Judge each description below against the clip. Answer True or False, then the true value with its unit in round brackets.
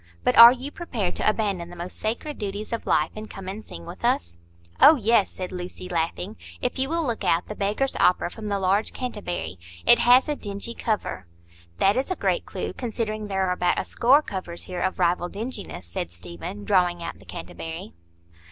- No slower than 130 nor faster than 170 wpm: False (200 wpm)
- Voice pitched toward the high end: True (200 Hz)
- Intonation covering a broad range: False (5.0 semitones)